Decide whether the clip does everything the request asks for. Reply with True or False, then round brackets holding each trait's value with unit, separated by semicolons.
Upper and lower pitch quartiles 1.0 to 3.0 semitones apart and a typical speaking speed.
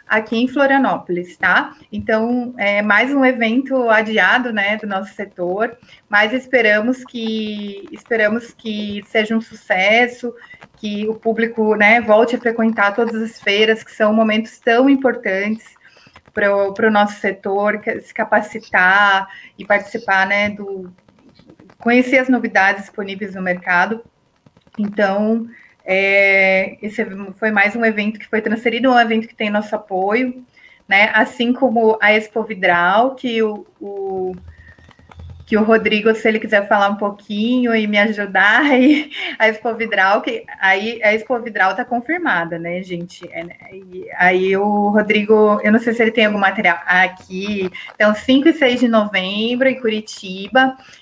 True (2.7 semitones; 150 wpm)